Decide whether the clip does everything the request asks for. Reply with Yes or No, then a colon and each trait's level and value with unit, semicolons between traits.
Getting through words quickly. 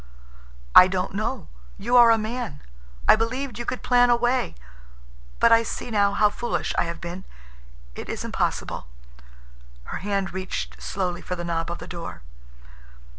No: average, 165 wpm